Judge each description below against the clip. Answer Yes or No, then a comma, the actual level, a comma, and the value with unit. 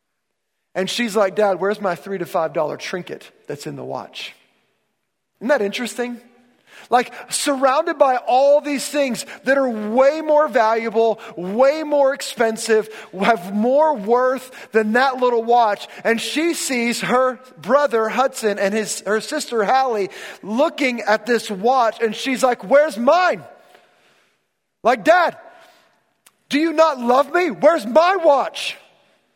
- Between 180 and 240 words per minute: No, average, 140 wpm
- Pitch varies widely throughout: No, average, 4.4 semitones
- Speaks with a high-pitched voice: Yes, high, 245 Hz